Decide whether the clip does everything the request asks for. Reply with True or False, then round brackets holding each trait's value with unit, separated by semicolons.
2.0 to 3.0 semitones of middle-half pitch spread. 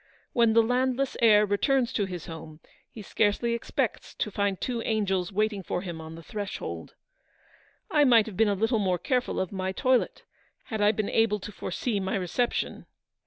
False (3.5 semitones)